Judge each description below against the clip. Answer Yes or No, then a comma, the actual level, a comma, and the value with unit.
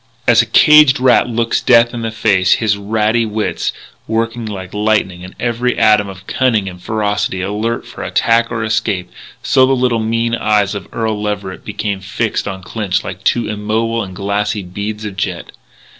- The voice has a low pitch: Yes, low, 110 Hz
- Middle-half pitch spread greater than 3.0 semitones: No, narrow, 2.4 semitones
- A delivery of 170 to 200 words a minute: Yes, average, 175 wpm